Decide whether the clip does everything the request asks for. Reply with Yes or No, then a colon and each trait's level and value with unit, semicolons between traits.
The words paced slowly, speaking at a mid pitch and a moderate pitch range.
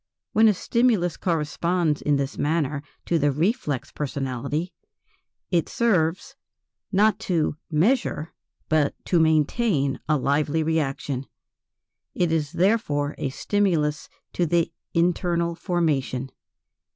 Yes: slow, 110 wpm; medium, 160 Hz; average, 3.5 semitones